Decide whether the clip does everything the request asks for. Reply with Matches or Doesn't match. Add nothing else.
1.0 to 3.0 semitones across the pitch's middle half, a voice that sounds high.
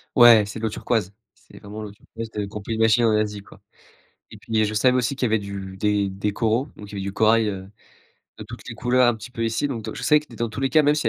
Doesn't match